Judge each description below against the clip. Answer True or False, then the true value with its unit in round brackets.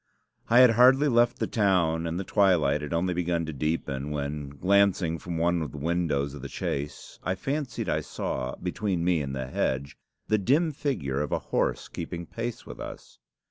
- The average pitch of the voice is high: False (85 Hz)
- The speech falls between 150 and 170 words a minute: False (190 wpm)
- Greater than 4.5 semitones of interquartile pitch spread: True (5.6 semitones)